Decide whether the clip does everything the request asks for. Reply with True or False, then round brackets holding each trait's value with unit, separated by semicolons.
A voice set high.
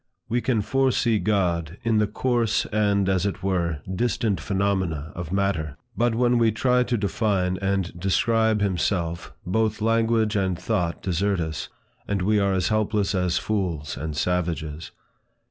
False (100 Hz)